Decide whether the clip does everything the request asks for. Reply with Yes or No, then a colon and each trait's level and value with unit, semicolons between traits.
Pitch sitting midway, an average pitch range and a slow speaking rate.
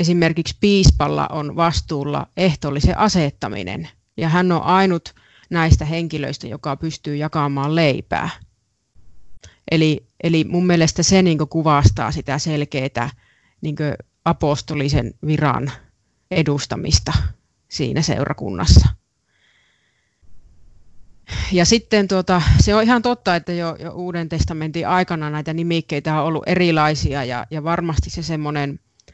No: medium, 155 Hz; average, 3.0 semitones; average, 110 wpm